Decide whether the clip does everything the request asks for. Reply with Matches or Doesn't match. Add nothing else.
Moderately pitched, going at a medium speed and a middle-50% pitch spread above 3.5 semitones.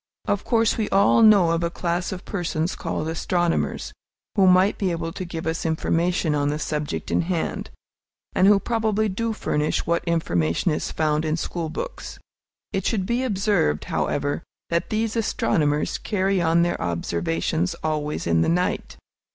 Matches